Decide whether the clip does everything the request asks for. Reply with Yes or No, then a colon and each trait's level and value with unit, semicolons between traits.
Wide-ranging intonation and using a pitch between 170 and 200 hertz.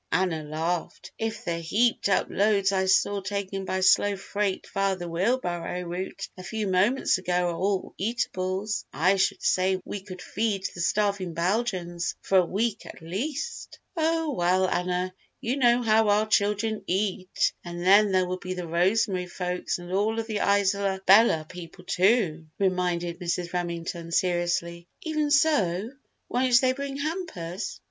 No: average, 3.2 semitones; high, 190 Hz